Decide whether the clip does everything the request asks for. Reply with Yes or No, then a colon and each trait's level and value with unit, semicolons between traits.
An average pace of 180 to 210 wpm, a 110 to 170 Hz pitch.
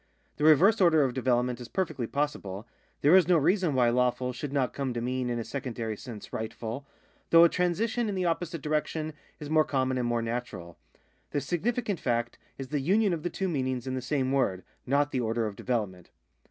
Yes: fast, 205 wpm; low, 135 Hz